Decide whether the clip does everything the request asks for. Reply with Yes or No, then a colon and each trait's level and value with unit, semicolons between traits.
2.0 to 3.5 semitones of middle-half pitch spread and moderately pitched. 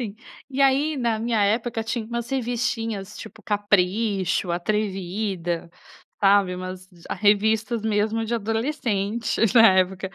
No: average, 3.0 semitones; high, 215 Hz